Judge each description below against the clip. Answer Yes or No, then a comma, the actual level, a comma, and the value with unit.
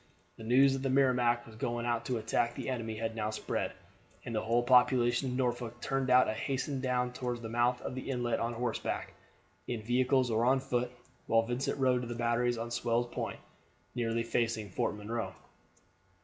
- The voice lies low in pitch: Yes, low, 120 Hz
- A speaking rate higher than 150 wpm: Yes, average, 190 wpm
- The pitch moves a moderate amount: No, narrow, 1.5 semitones